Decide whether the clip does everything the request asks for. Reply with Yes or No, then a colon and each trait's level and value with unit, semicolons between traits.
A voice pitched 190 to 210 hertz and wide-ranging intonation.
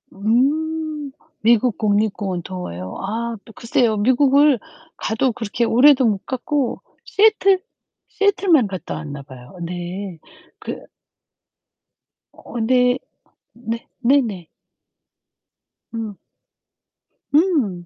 No: high, 230 Hz; wide, 6.1 semitones